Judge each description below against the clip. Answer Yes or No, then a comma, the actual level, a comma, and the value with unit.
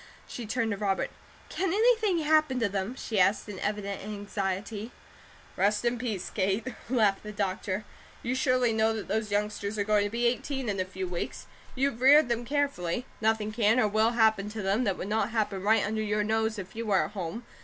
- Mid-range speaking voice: No, high, 215 Hz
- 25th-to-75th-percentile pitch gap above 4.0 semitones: No, average, 2.9 semitones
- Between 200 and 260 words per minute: Yes, fast, 205 wpm